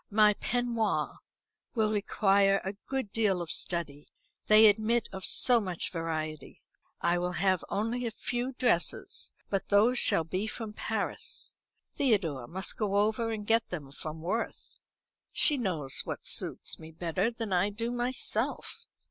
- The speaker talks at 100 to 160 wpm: Yes, average, 150 wpm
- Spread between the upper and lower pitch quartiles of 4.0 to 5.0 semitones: Yes, average, 4.5 semitones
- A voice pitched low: No, high, 205 Hz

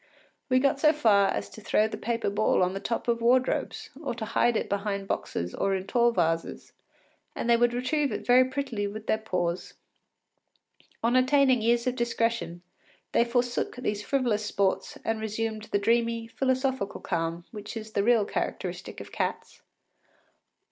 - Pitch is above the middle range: Yes, high, 230 Hz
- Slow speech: No, average, 170 wpm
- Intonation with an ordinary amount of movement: Yes, average, 3.3 semitones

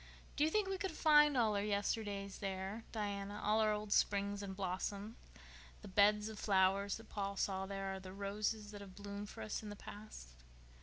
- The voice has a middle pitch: No, high, 205 Hz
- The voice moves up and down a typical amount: No, narrow, 1.4 semitones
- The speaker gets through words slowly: No, average, 195 wpm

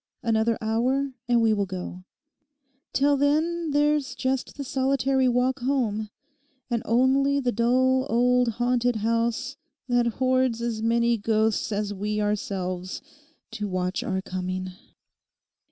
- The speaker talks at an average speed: No, slow, 125 wpm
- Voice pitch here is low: No, high, 235 Hz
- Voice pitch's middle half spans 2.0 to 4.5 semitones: Yes, average, 3.5 semitones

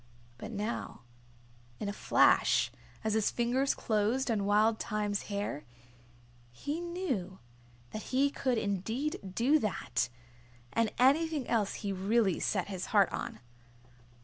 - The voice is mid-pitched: No, high, 220 Hz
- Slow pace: Yes, slow, 125 wpm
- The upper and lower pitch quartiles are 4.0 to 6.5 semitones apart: Yes, average, 4.3 semitones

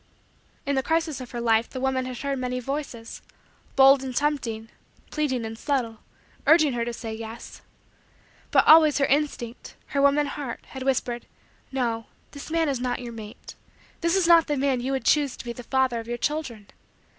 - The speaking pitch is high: Yes, very high, 260 Hz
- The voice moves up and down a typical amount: Yes, average, 3.3 semitones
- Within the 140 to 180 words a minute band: No, average, 190 wpm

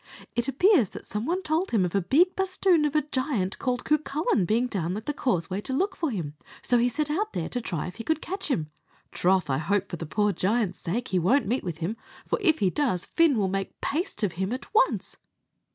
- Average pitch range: No, wide, 8.3 semitones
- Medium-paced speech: No, fast, 240 wpm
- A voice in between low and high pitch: No, high, 240 Hz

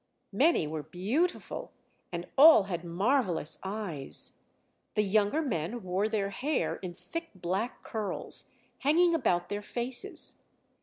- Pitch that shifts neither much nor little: No, wide, 6.9 semitones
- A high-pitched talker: Yes, high, 205 Hz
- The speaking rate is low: Yes, slow, 120 wpm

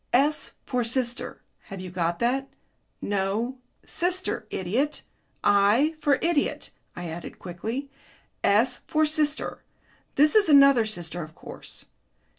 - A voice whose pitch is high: Yes, high, 240 Hz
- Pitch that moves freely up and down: Yes, wide, 7.1 semitones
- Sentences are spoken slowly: Yes, slow, 120 wpm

